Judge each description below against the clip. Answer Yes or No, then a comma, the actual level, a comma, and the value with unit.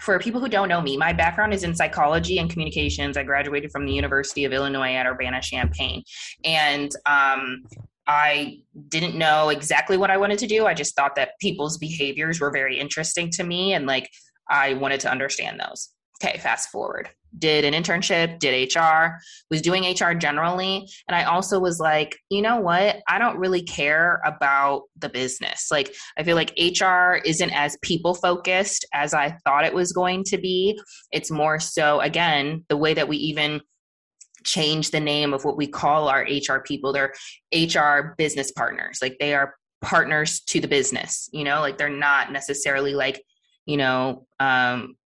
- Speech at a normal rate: Yes, average, 180 wpm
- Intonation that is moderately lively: Yes, average, 3.8 semitones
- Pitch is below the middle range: No, medium, 150 Hz